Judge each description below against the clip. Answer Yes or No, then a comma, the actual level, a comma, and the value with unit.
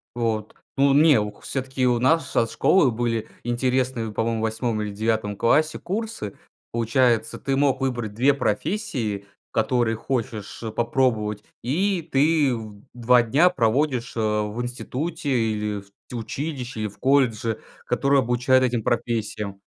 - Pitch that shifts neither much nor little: Yes, average, 3.4 semitones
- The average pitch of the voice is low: Yes, low, 120 Hz